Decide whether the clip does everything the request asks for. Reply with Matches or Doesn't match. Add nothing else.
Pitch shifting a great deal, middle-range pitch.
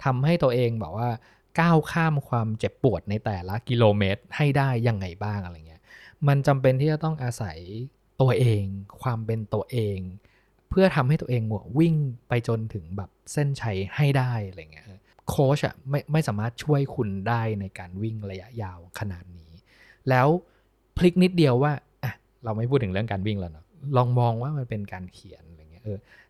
Doesn't match